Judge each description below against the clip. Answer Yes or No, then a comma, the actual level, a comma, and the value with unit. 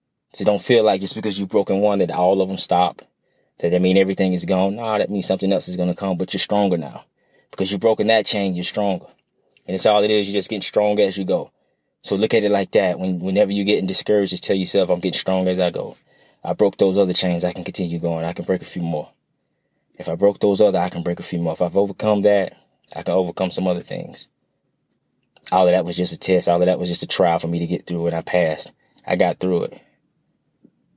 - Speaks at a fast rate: Yes, fast, 260 wpm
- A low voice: Yes, very low, 95 Hz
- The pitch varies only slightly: Yes, narrow, 2.1 semitones